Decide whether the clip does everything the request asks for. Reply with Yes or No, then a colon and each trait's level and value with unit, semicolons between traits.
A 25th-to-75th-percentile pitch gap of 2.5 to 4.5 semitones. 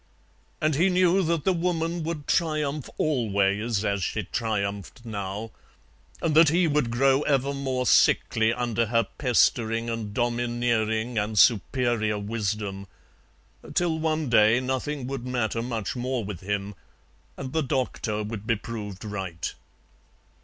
No: average, 4.9 semitones